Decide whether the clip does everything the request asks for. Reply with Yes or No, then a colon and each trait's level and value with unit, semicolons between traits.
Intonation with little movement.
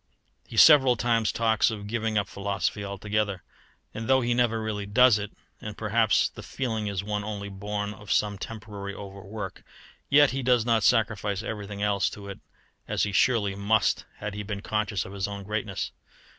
Yes: narrow, 1.9 semitones